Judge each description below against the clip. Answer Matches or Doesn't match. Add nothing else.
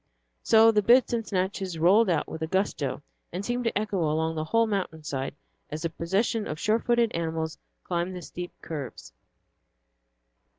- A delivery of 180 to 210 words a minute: Doesn't match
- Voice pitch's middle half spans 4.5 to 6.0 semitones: Matches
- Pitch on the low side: Doesn't match